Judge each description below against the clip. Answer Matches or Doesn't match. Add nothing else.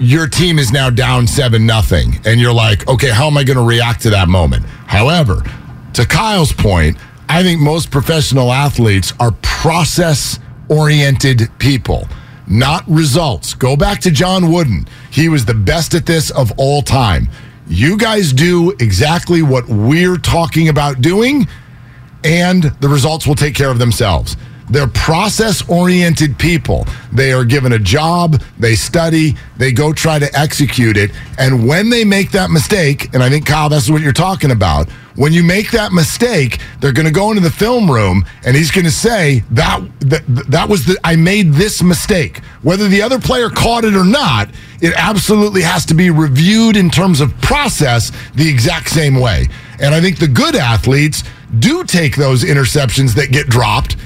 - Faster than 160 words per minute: Matches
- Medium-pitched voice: Matches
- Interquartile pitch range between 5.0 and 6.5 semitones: Matches